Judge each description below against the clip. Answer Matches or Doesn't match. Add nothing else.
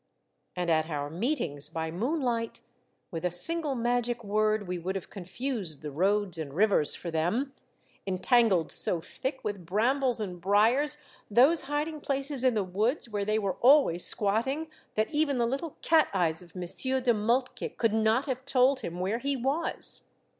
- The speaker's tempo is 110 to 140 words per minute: Doesn't match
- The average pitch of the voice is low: Doesn't match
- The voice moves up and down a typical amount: Doesn't match